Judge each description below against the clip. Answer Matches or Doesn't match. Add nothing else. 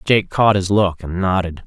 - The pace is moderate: Doesn't match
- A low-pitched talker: Matches